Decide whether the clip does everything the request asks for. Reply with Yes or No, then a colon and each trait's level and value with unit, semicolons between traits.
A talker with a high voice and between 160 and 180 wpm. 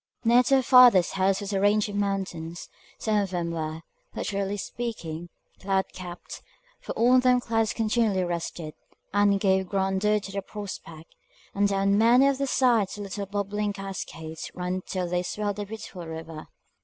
Yes: high, 200 Hz; average, 170 wpm